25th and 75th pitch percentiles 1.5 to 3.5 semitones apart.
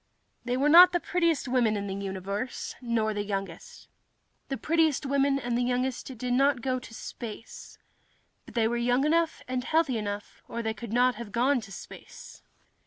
No: average, 3.9 semitones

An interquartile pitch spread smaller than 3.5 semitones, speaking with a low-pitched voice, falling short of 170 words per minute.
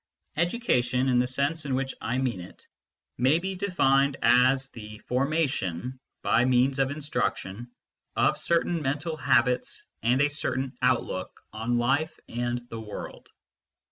Yes: average, 3.0 semitones; low, 130 Hz; average, 140 wpm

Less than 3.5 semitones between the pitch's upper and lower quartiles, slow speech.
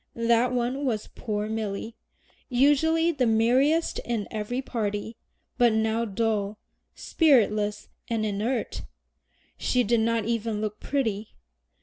Yes: average, 2.8 semitones; slow, 115 wpm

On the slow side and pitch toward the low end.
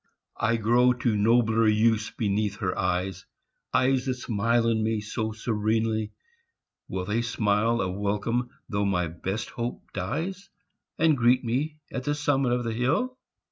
No: average, 150 wpm; low, 115 Hz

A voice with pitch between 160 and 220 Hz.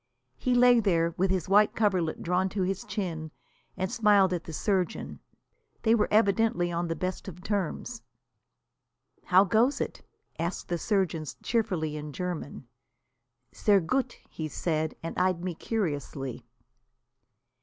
Yes: medium, 185 Hz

